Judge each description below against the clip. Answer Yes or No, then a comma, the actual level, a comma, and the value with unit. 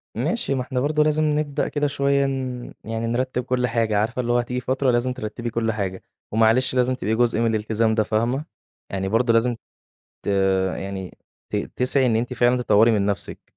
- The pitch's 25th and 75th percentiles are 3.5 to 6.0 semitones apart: No, narrow, 2.5 semitones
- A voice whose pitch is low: Yes, low, 120 Hz